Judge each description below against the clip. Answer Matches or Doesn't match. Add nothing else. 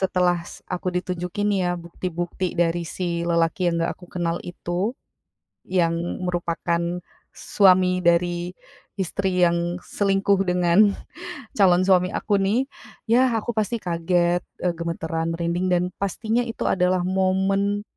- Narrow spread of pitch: Matches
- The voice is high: Doesn't match